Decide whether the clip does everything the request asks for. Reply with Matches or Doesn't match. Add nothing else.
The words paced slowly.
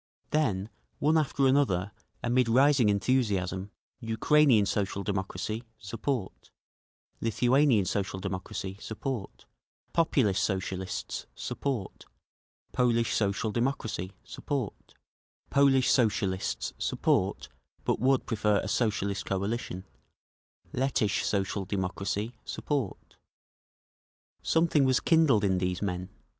Matches